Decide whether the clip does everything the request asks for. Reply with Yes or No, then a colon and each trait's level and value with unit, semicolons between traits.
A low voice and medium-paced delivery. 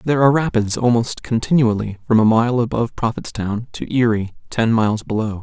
Yes: low, 115 Hz; average, 165 wpm